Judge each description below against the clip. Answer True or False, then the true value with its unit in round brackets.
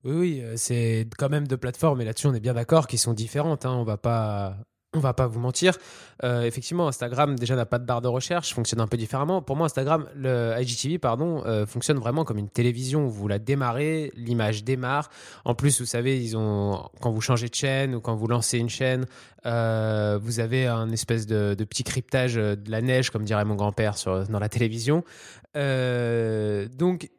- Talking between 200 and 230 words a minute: True (205 wpm)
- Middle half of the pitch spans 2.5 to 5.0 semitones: True (3.2 semitones)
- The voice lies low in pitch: True (120 Hz)